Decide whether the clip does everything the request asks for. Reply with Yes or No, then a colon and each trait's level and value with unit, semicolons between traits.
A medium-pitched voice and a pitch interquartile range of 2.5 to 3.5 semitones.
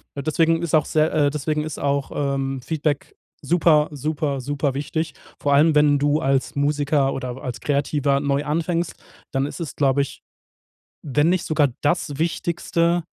No: medium, 145 Hz; narrow, 2.1 semitones